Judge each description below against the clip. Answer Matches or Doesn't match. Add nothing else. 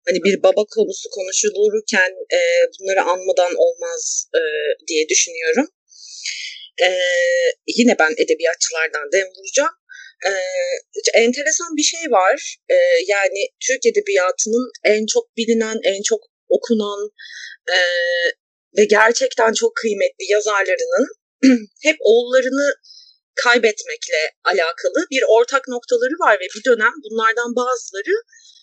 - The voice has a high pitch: Matches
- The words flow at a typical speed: Matches